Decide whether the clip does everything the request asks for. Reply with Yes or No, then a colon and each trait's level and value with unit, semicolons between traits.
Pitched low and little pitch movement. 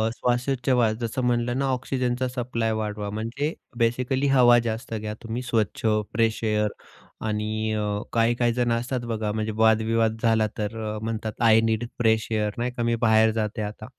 Yes: low, 115 Hz; narrow, 1.9 semitones